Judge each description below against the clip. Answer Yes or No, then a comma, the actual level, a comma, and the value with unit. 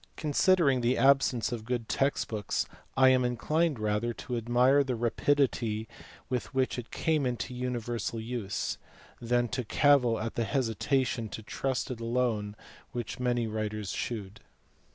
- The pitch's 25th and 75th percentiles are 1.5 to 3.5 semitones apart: Yes, narrow, 2.6 semitones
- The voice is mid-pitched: No, low, 120 Hz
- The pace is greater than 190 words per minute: No, average, 150 wpm